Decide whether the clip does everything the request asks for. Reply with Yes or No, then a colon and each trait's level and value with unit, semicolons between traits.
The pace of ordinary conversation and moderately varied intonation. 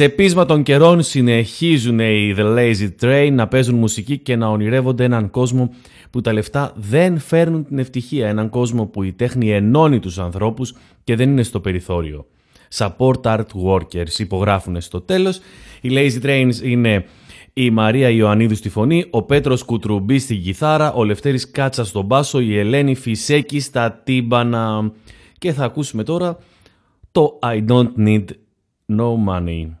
Yes: average, 155 wpm; average, 4.2 semitones